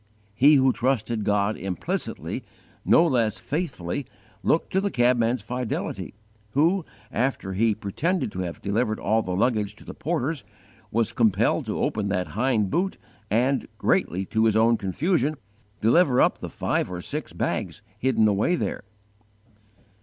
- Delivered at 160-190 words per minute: No, average, 150 wpm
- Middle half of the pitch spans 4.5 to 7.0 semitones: Yes, average, 4.9 semitones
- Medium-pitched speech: No, low, 115 Hz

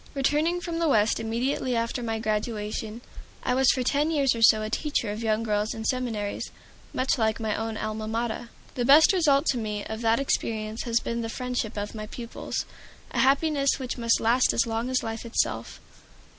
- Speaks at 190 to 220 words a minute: Yes, average, 195 wpm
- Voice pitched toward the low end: No, high, 230 Hz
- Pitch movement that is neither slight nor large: Yes, average, 3.1 semitones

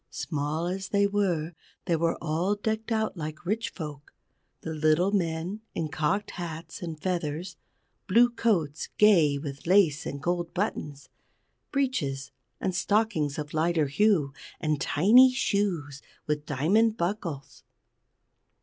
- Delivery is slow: Yes, slow, 130 wpm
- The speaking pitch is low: No, medium, 170 Hz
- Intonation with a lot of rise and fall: No, average, 5.0 semitones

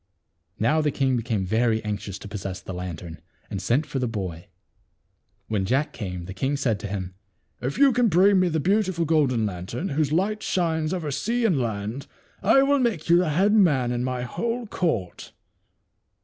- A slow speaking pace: No, average, 200 wpm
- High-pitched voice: No, low, 135 Hz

